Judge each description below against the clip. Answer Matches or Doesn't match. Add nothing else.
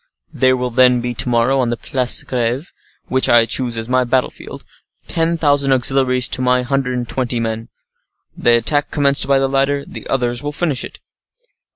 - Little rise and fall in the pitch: Matches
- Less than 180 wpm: Doesn't match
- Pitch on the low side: Matches